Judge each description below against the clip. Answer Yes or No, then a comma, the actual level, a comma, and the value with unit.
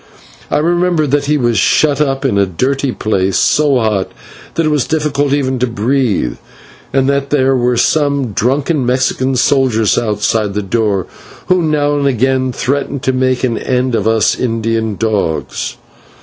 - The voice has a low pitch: Yes, low, 130 Hz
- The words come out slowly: No, average, 165 wpm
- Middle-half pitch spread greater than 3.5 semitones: Yes, average, 4.0 semitones